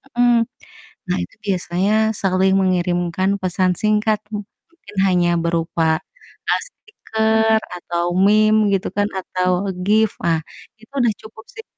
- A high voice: Yes, high, 195 Hz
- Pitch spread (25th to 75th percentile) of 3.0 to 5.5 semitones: Yes, average, 3.4 semitones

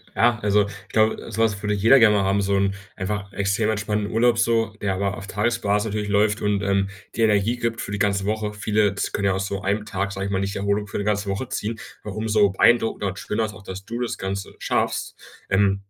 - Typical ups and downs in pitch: No, narrow, 1.7 semitones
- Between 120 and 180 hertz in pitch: No, low, 105 Hz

